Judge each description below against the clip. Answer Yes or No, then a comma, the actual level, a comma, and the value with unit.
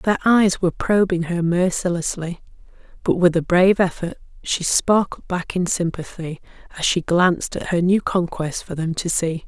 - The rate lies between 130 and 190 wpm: Yes, average, 170 wpm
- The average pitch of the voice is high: No, medium, 175 Hz